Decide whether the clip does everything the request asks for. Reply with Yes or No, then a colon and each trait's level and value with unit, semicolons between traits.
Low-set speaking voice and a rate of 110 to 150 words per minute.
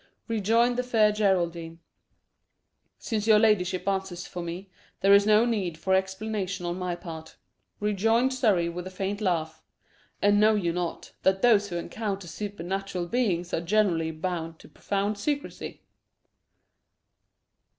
No: high, 195 Hz; average, 140 wpm